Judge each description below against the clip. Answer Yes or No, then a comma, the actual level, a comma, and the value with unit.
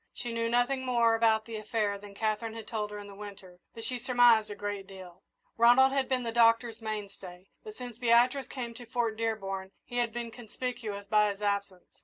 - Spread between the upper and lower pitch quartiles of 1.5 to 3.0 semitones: Yes, average, 2.7 semitones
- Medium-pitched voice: No, high, 225 Hz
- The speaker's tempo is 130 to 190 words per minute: No, fast, 205 wpm